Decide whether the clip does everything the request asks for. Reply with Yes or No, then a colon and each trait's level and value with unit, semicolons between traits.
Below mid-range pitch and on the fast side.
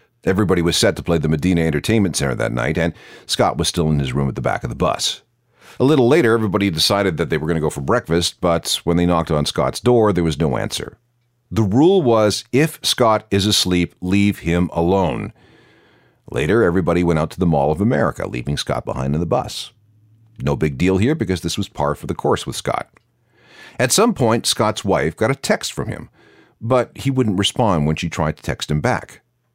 Yes: very low, 90 Hz; fast, 215 wpm